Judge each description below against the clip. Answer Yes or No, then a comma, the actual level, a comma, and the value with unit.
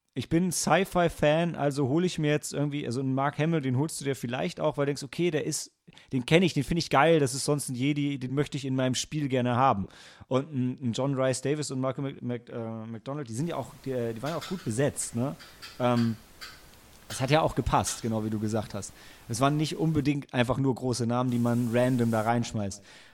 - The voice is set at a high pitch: No, low, 135 Hz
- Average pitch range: Yes, average, 3.4 semitones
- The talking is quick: Yes, fast, 230 wpm